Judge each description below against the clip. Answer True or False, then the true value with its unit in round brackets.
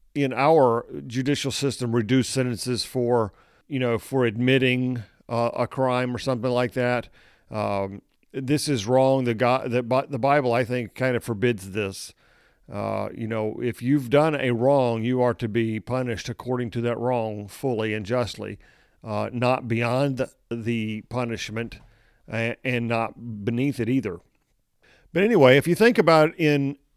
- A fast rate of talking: False (160 wpm)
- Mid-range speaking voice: False (125 Hz)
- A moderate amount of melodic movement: False (2.3 semitones)